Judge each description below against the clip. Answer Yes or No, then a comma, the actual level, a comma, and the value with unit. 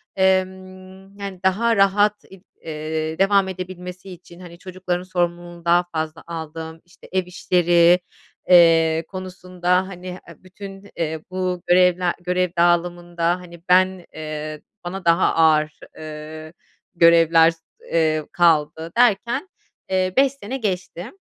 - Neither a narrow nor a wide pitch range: No, narrow, 2.1 semitones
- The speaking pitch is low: No, medium, 180 Hz